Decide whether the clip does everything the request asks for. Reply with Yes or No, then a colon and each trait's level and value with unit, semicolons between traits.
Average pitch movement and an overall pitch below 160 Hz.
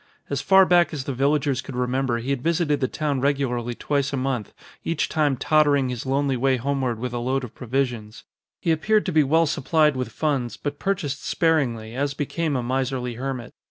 Yes: average, 3.0 semitones; low, 135 Hz